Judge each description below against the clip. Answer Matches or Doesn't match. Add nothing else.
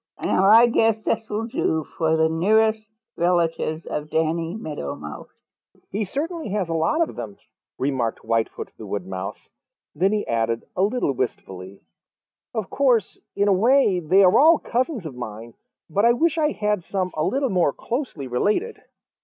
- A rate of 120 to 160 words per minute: Doesn't match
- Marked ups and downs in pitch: Matches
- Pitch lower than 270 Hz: Matches